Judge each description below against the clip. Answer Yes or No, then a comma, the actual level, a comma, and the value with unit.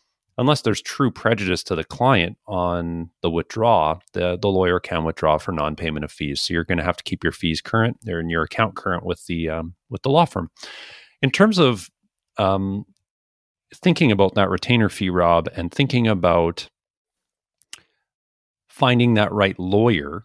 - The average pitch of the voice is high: No, very low, 90 Hz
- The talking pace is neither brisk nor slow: Yes, average, 175 wpm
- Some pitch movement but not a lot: Yes, average, 4.6 semitones